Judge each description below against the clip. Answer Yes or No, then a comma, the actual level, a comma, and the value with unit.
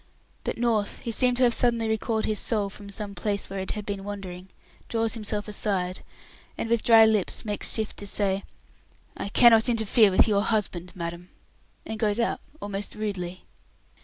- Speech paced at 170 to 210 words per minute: Yes, average, 175 wpm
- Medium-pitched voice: No, high, 210 Hz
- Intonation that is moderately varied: No, narrow, 2.2 semitones